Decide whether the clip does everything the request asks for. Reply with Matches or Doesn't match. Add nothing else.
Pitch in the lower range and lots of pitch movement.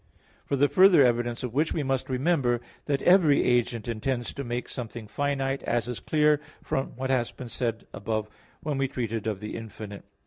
Doesn't match